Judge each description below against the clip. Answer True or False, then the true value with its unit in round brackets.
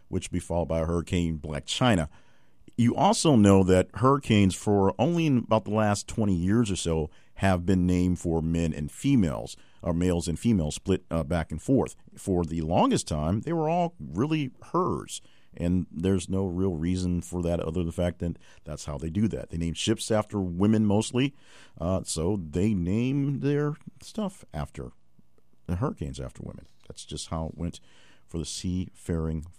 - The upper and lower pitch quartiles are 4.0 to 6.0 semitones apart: True (4.6 semitones)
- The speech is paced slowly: False (185 wpm)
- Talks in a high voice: False (90 Hz)